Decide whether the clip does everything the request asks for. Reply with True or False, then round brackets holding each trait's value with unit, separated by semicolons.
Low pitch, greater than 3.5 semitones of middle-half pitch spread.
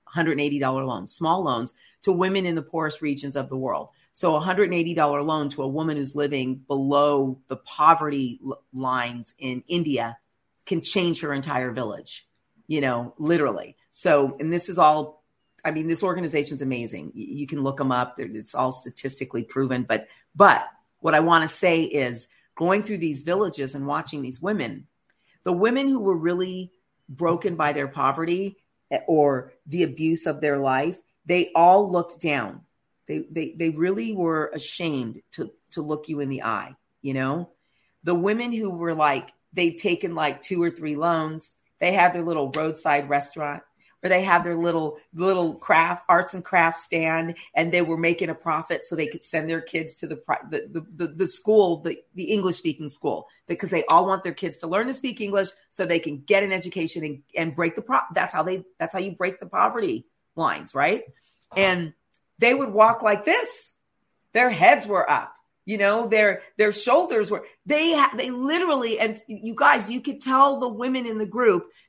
False (165 Hz; 4.7 semitones)